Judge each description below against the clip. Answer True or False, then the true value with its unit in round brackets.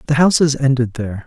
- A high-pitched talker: False (135 Hz)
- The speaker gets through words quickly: False (190 wpm)